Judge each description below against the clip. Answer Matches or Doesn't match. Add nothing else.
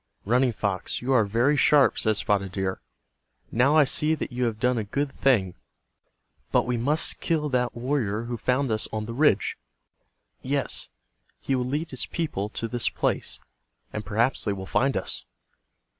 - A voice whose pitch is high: Doesn't match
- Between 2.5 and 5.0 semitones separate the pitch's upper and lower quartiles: Matches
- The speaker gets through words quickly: Doesn't match